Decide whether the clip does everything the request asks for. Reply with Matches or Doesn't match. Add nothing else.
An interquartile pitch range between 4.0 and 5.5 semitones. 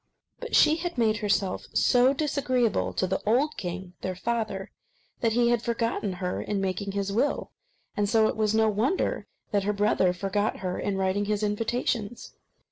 Doesn't match